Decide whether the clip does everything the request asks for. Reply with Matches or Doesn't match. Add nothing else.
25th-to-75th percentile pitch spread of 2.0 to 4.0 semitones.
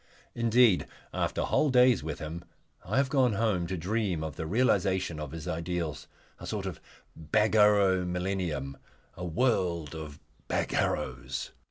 Doesn't match